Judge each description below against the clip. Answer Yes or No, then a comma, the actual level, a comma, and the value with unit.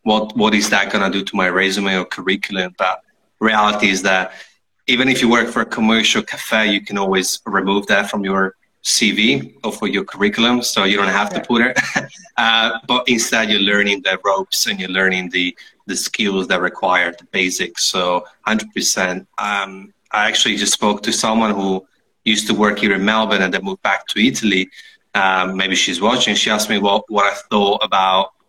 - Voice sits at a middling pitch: No, low, 100 Hz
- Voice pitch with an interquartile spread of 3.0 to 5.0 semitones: No, narrow, 2.4 semitones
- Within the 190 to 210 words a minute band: Yes, average, 200 wpm